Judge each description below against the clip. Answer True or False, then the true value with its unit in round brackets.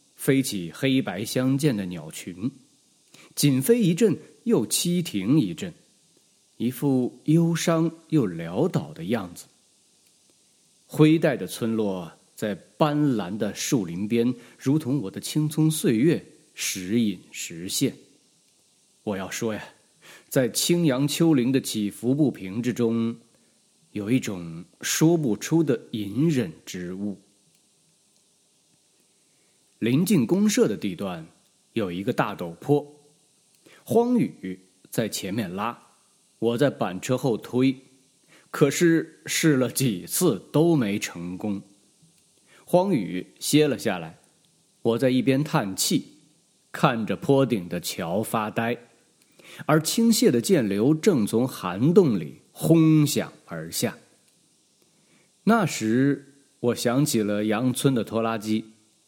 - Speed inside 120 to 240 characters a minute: True (165 characters per minute)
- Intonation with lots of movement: True (6.0 semitones)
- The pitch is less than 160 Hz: True (135 Hz)